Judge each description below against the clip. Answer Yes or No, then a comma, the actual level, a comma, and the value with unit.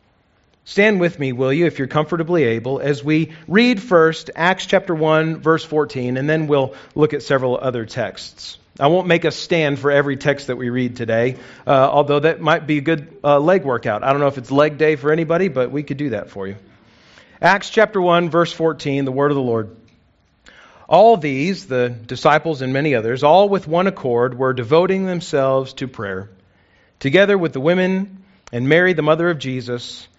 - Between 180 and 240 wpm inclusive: Yes, average, 200 wpm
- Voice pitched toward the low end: No, medium, 145 Hz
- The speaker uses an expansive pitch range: No, average, 4.7 semitones